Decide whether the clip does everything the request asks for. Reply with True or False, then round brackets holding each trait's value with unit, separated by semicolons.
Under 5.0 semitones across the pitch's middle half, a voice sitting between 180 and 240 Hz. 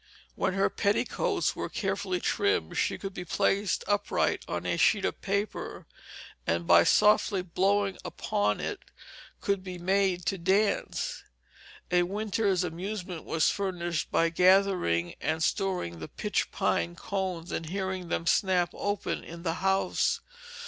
True (2.8 semitones; 185 Hz)